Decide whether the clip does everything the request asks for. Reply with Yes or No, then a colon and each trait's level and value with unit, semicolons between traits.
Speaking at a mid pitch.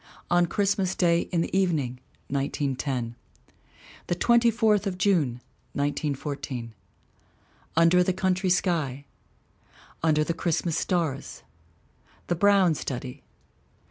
Yes: medium, 170 Hz